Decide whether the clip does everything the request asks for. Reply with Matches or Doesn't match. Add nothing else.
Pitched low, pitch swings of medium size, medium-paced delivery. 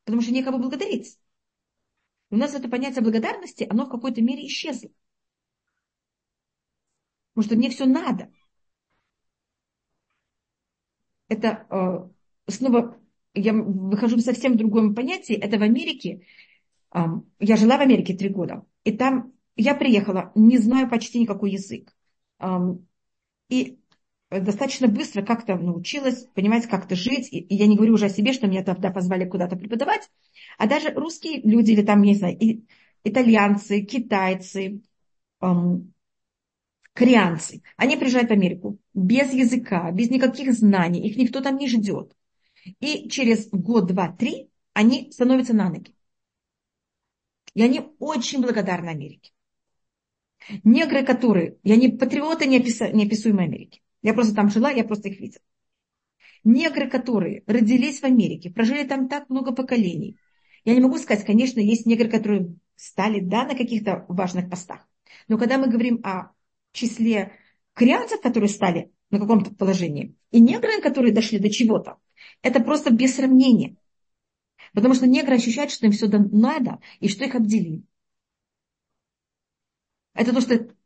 Doesn't match